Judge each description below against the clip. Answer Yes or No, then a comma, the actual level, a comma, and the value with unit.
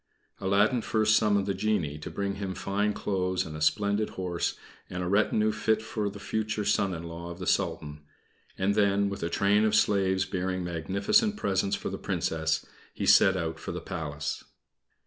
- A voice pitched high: No, low, 100 Hz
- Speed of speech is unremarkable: Yes, average, 185 wpm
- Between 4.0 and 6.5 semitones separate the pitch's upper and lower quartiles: No, average, 3.1 semitones